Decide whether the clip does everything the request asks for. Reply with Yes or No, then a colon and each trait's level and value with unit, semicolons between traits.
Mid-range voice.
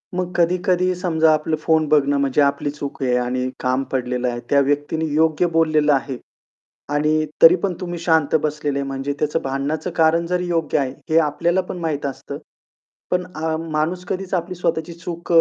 Yes: medium, 155 Hz